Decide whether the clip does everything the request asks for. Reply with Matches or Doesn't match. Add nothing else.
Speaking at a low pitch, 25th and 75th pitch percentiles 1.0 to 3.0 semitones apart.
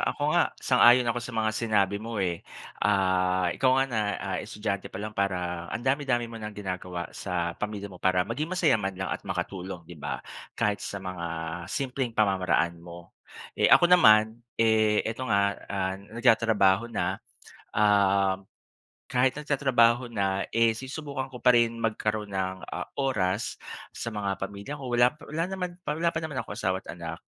Doesn't match